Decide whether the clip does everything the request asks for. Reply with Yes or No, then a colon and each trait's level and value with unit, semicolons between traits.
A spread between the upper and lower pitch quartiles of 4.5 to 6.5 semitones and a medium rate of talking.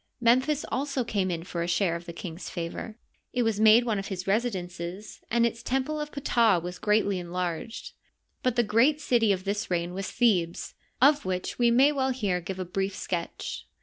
Yes: average, 5.1 semitones; average, 195 wpm